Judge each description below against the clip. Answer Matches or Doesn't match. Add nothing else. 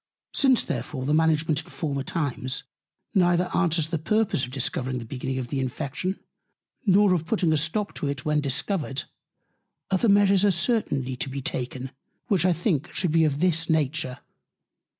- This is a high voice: Doesn't match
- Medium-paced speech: Matches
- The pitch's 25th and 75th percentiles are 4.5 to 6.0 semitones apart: Matches